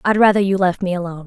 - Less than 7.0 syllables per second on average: No, 7.7 syllables/s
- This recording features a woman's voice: Yes, female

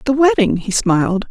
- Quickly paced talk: No, average, 185 wpm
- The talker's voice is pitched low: No, high, 235 Hz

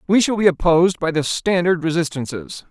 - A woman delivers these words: No, male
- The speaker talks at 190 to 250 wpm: No, average, 180 wpm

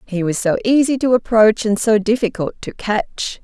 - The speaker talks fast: No, average, 190 wpm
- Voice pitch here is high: Yes, high, 220 Hz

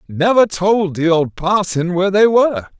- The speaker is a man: Yes, male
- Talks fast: No, average, 170 wpm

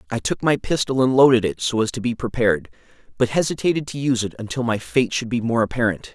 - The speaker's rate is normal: No, fast, 235 wpm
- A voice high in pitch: No, low, 120 Hz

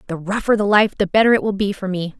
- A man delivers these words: No, female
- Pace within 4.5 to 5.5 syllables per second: No, 6.7 syllables/s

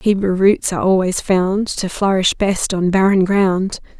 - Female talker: Yes, female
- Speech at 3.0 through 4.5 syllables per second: Yes, 4.2 syllables/s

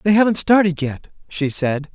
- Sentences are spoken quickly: No, average, 185 wpm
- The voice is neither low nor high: Yes, medium, 170 Hz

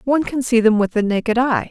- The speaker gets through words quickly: Yes, fast, 280 wpm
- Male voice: No, female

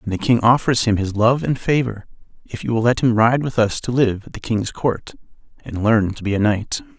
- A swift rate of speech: Yes, fast, 250 wpm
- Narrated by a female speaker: No, male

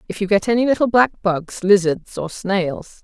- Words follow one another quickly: No, average, 180 wpm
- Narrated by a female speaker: Yes, female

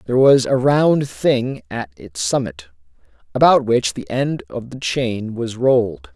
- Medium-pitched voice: No, low, 115 Hz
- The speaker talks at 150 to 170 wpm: Yes, average, 165 wpm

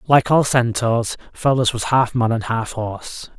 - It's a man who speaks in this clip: Yes, male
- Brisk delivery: No, average, 175 wpm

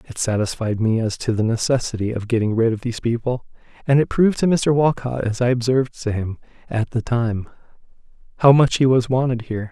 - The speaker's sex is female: No, male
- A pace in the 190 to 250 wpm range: Yes, fast, 205 wpm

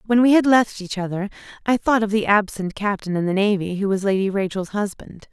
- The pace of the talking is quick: Yes, fast, 225 wpm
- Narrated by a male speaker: No, female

